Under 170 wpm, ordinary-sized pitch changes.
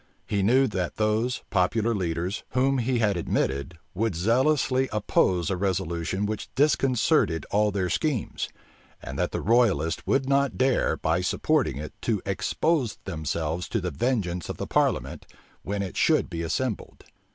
No: average, 150 wpm; wide, 6.2 semitones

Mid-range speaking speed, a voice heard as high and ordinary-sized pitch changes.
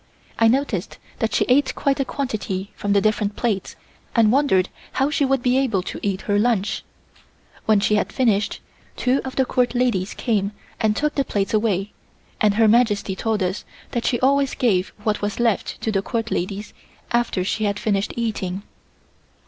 Yes: average, 180 wpm; high, 220 Hz; average, 3.8 semitones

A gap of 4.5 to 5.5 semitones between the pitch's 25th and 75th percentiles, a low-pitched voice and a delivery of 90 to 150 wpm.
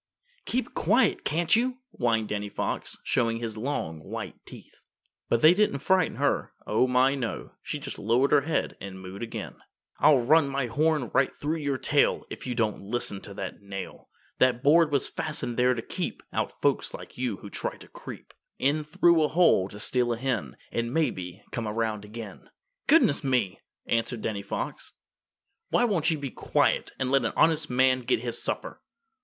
No: average, 5.1 semitones; low, 125 Hz; average, 180 wpm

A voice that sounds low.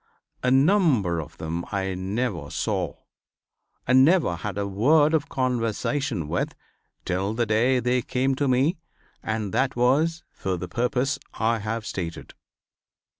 Yes: low, 120 Hz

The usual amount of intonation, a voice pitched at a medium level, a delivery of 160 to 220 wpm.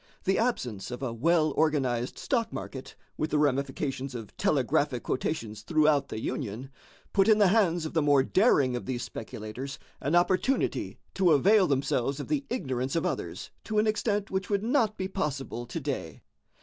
No: wide, 6.7 semitones; medium, 145 Hz; average, 175 wpm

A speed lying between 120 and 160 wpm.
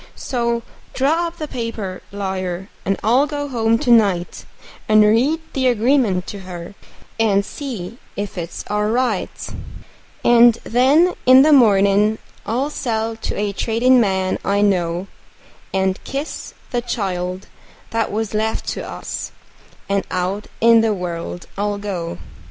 Yes: average, 140 wpm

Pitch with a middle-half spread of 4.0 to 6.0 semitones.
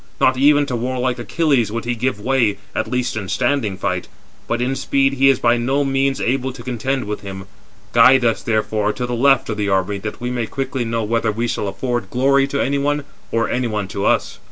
No: average, 3.6 semitones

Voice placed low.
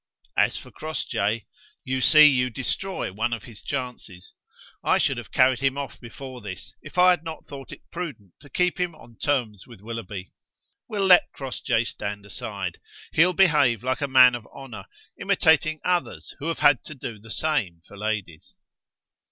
Yes: low, 130 Hz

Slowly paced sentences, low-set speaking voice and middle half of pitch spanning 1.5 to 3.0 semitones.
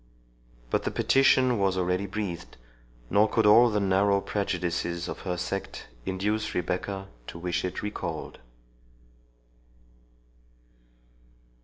Yes: slow, 110 wpm; very low, 95 Hz; narrow, 2.5 semitones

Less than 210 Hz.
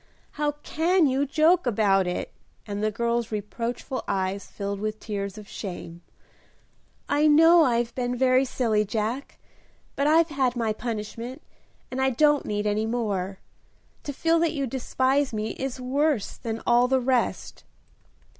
No: high, 245 Hz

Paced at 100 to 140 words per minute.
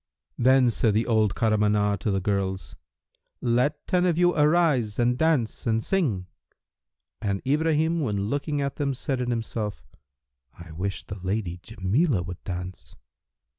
No: average, 150 wpm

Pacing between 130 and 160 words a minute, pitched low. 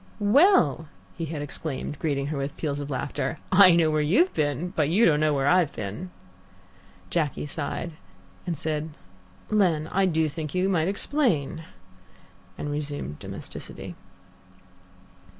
No: average, 140 wpm; medium, 155 Hz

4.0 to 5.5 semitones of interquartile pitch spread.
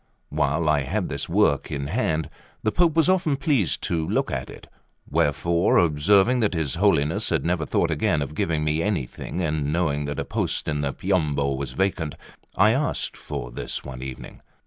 Yes: average, 5.2 semitones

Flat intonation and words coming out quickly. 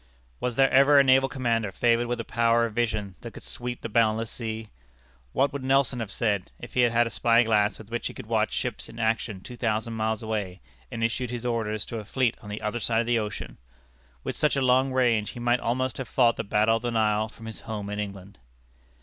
Yes: narrow, 2.1 semitones; fast, 240 wpm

